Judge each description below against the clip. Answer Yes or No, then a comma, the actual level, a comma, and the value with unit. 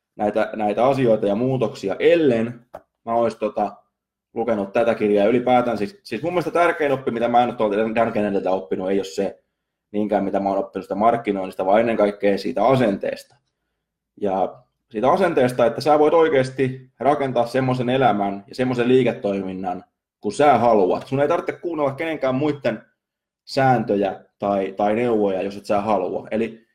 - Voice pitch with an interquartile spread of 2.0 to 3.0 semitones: No, average, 4.2 semitones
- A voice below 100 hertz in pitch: No, low, 115 Hz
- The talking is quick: Yes, fast, 160 wpm